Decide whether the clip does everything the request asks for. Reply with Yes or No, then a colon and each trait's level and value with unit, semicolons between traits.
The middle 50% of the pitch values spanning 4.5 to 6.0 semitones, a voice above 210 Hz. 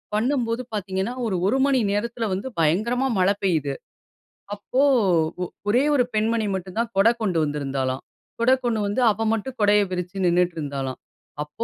No: average, 4.8 semitones; high, 205 Hz